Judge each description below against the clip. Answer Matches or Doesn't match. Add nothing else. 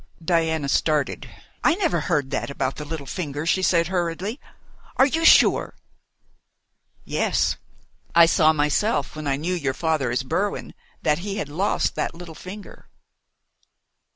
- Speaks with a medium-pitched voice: Matches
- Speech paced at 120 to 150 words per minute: Matches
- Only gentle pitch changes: Doesn't match